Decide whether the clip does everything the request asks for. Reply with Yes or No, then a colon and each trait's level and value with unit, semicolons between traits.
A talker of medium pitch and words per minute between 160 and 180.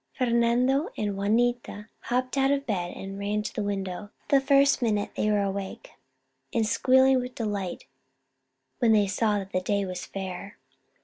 No: high, 210 Hz; average, 165 wpm